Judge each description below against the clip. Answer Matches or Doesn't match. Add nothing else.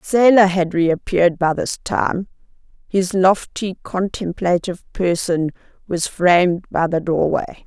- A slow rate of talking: Matches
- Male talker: Doesn't match